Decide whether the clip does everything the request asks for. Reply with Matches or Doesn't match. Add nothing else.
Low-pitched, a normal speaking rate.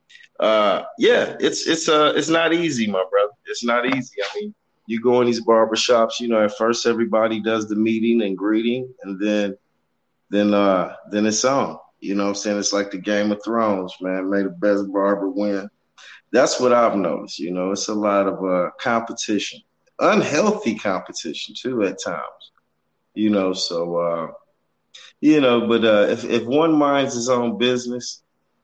Matches